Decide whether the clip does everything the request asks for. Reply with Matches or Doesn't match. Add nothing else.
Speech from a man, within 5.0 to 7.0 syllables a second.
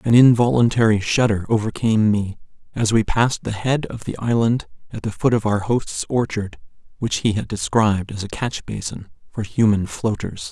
Matches